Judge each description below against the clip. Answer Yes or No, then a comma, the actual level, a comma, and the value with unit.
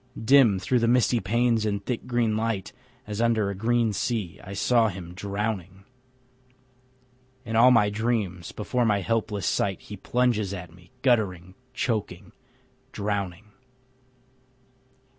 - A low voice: Yes, low, 105 Hz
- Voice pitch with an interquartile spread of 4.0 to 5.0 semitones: No, average, 3.1 semitones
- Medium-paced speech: No, slow, 130 wpm